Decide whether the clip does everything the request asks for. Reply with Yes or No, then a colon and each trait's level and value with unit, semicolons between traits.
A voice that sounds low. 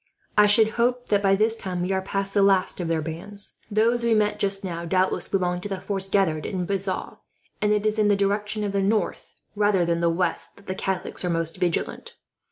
No: high, 195 Hz